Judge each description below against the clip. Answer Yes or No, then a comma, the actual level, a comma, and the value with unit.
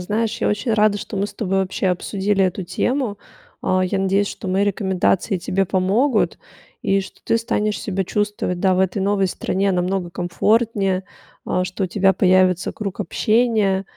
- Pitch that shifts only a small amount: Yes, narrow, 1.9 semitones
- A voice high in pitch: Yes, high, 195 Hz